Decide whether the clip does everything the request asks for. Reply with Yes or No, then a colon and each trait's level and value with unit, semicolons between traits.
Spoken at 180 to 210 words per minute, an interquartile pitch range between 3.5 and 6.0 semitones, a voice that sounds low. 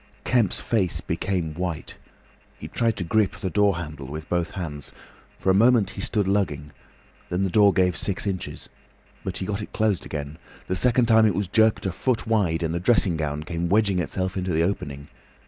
Yes: average, 200 wpm; average, 3.9 semitones; very low, 95 Hz